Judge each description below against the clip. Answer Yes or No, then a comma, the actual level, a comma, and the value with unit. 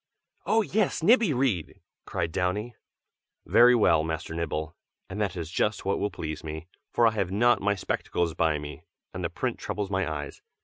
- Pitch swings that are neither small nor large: No, wide, 6.0 semitones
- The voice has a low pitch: Yes, very low, 95 Hz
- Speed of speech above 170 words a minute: Yes, average, 180 wpm